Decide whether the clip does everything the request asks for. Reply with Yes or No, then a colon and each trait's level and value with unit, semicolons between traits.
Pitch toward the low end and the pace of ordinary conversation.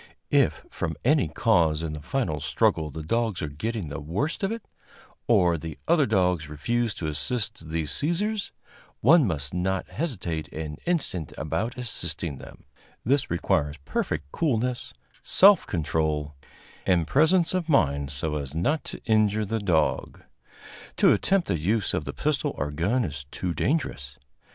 Yes: very low, 90 Hz; average, 155 wpm